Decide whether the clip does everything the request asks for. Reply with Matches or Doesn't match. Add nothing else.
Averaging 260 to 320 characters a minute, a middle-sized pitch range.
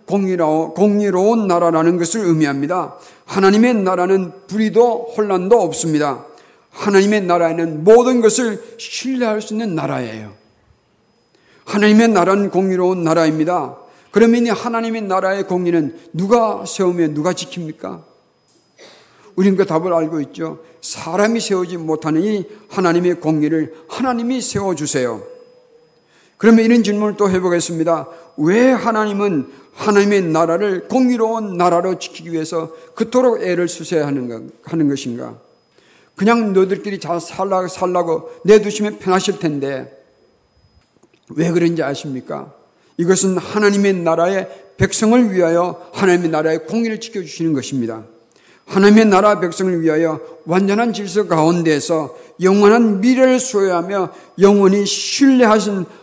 Matches